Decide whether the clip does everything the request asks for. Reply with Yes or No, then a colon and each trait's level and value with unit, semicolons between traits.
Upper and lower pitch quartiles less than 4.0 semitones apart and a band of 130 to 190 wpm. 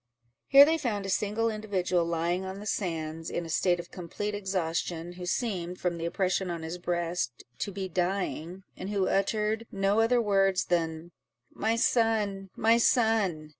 Yes: average, 3.4 semitones; average, 170 wpm